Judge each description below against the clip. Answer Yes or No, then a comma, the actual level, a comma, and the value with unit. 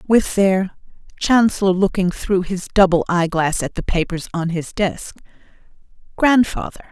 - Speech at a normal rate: No, slow, 120 wpm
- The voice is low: No, medium, 185 Hz